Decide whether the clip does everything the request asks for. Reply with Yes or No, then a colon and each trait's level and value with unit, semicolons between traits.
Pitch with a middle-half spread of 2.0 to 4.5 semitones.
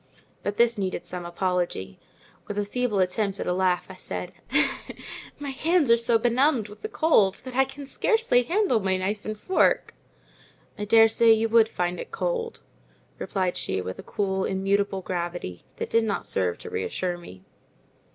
No: average, 4.9 semitones